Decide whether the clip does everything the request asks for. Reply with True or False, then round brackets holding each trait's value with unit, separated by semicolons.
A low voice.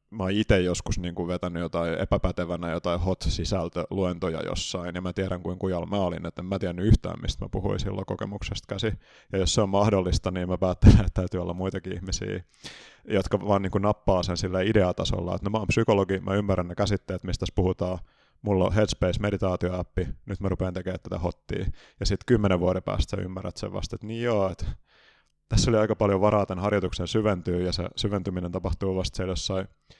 True (95 Hz)